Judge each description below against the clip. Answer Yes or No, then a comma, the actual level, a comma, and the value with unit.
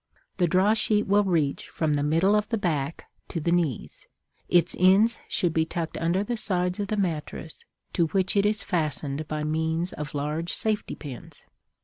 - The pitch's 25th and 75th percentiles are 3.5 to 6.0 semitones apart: Yes, average, 4.3 semitones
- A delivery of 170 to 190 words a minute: Yes, average, 180 wpm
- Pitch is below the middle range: No, medium, 170 Hz